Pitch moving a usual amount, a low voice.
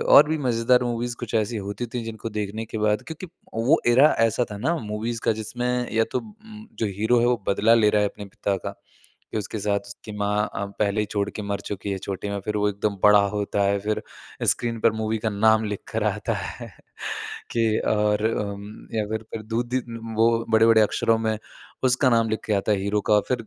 No: narrow, 2.2 semitones; low, 110 Hz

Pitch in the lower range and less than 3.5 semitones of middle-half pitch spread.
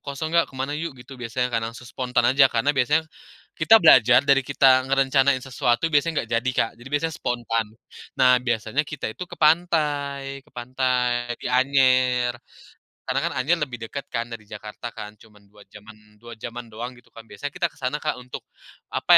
Yes: low, 130 Hz; average, 3.0 semitones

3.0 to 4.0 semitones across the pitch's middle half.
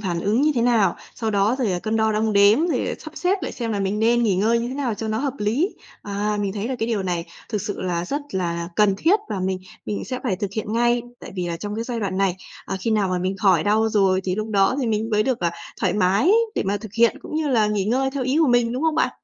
Yes: average, 3.6 semitones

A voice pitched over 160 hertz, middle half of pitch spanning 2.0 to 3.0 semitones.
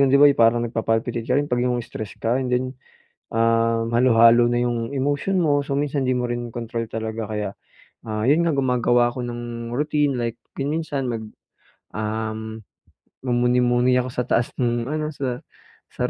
No: low, 120 Hz; narrow, 2.5 semitones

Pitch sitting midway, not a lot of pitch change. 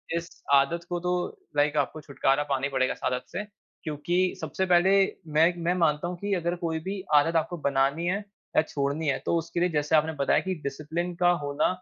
No: medium, 160 Hz; average, 3.4 semitones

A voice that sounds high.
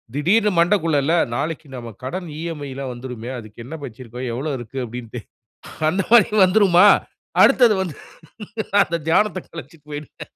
No: medium, 150 Hz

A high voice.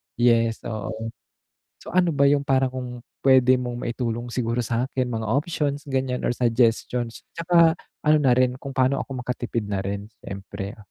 No: low, 125 Hz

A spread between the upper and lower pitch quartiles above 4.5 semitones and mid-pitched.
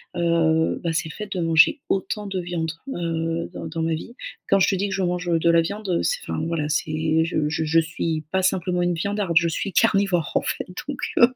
No: average, 2.9 semitones; medium, 170 Hz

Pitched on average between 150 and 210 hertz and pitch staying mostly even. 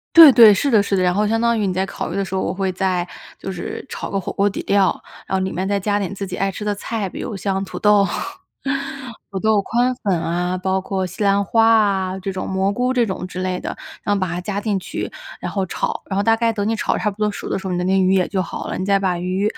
Yes: high, 195 Hz; narrow, 1.9 semitones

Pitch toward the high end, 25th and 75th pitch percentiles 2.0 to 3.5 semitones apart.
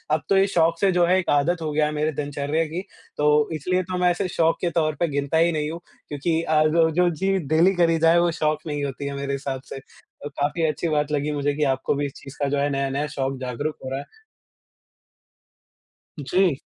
No: medium, 150 Hz; average, 2.9 semitones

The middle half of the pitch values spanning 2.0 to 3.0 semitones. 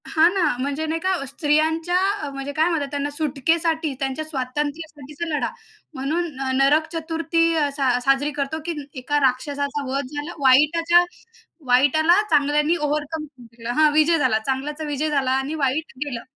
Yes: average, 2.7 semitones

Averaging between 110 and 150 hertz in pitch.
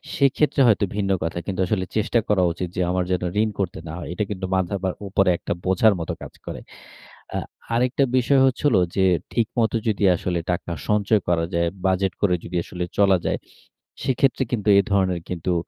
No: very low, 95 Hz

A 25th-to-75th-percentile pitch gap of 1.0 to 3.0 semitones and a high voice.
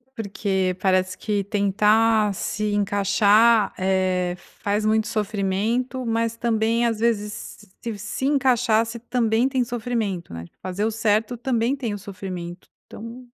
Yes: average, 2.7 semitones; high, 215 Hz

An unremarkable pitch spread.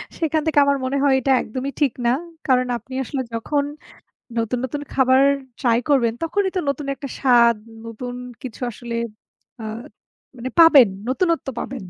Yes: average, 3.0 semitones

